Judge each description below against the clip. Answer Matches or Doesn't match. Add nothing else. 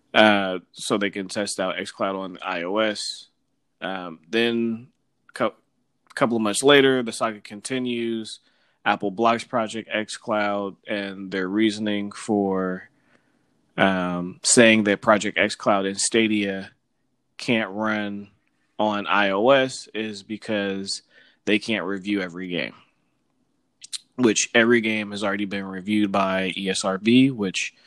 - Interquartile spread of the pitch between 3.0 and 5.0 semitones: Doesn't match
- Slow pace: Matches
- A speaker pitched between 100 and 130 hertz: Matches